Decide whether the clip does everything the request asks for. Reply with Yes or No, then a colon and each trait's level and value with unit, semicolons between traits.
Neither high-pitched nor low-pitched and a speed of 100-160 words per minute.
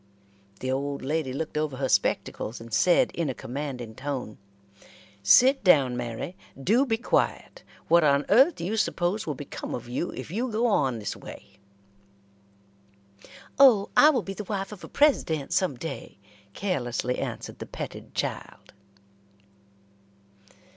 Yes: medium, 155 Hz; average, 145 wpm